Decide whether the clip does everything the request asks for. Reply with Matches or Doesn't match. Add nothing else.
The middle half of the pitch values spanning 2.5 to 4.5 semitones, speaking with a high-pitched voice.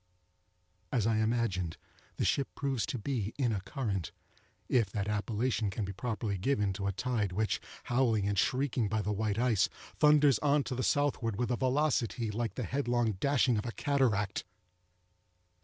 Doesn't match